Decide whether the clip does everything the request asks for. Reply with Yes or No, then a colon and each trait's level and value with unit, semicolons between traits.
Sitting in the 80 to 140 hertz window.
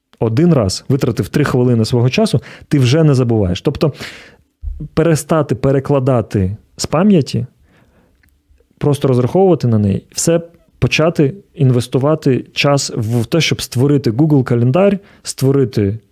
Yes: low, 135 Hz